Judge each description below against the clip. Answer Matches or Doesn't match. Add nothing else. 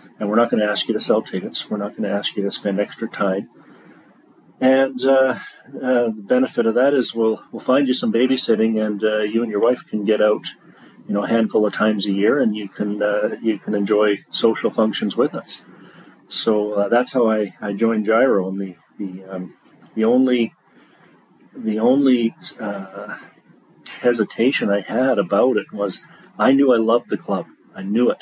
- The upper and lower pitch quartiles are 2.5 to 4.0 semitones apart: Matches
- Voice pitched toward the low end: Matches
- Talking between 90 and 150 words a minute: Doesn't match